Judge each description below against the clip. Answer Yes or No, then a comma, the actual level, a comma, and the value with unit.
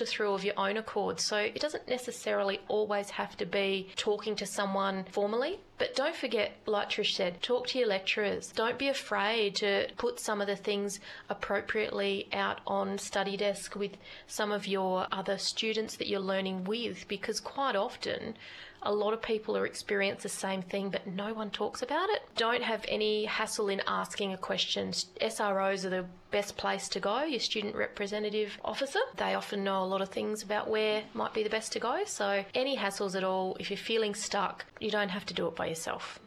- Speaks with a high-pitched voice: Yes, high, 205 Hz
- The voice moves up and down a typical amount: No, narrow, 1.8 semitones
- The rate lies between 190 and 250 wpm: Yes, average, 200 wpm